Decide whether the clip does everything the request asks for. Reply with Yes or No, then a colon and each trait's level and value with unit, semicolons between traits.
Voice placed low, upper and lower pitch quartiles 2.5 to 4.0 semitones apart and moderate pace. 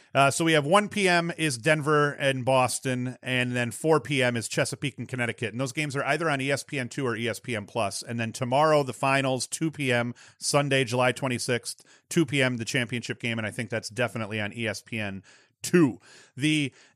Yes: low, 130 Hz; average, 3.6 semitones; average, 180 wpm